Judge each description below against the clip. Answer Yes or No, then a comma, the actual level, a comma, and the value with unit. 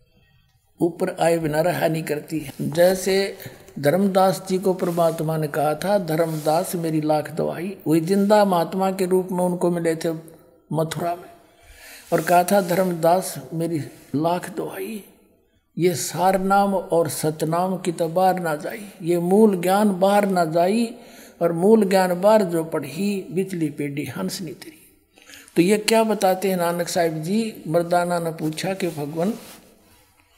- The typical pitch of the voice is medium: Yes, medium, 175 Hz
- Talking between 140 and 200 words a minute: Yes, average, 150 wpm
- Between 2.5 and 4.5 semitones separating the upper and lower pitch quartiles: Yes, average, 2.8 semitones